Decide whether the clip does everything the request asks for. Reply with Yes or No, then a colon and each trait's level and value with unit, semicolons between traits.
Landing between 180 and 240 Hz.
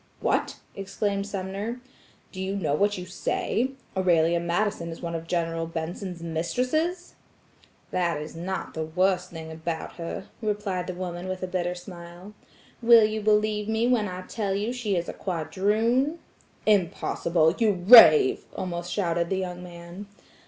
Yes: medium, 185 Hz